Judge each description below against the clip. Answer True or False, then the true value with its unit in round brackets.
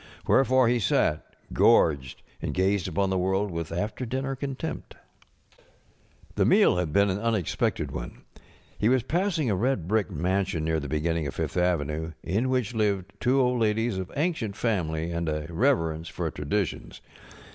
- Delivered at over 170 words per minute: False (160 wpm)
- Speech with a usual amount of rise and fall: False (6.5 semitones)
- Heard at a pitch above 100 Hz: False (95 Hz)